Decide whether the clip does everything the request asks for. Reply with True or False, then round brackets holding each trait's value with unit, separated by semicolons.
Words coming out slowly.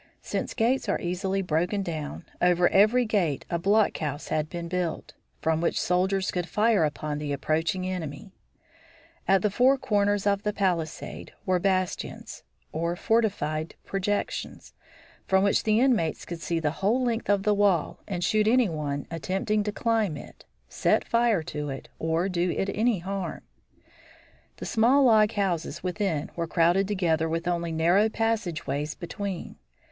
False (160 wpm)